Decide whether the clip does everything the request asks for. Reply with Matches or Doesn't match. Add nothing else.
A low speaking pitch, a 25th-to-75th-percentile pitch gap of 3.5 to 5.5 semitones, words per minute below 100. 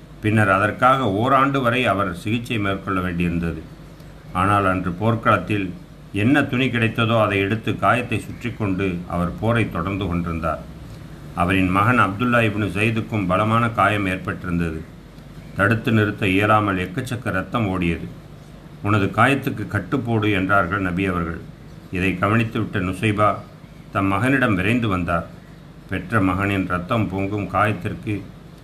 Doesn't match